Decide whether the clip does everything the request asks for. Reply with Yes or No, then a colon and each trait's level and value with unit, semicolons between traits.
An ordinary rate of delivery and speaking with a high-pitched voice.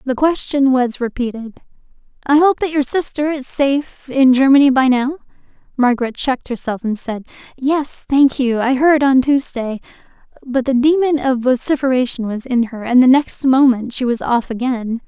Yes: average, 170 wpm; very high, 260 Hz